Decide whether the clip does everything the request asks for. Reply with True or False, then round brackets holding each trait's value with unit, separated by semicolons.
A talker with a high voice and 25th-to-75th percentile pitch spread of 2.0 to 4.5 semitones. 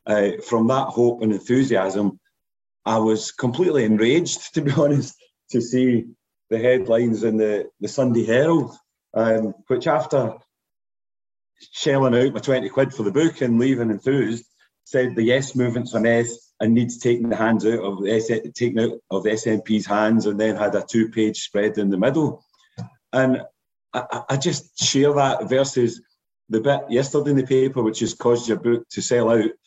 False (115 Hz; 3.0 semitones)